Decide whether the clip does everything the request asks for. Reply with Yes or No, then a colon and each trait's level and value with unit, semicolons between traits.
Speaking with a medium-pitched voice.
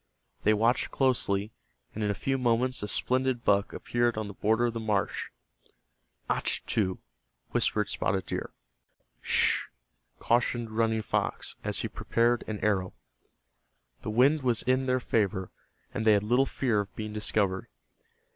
No: low, 110 Hz